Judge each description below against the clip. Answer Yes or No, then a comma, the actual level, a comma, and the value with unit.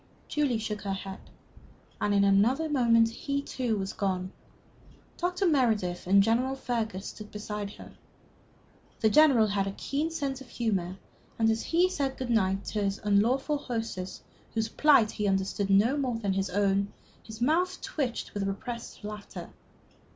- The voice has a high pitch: Yes, high, 220 Hz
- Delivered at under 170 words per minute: Yes, average, 160 wpm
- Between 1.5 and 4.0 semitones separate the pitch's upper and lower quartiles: No, average, 5.0 semitones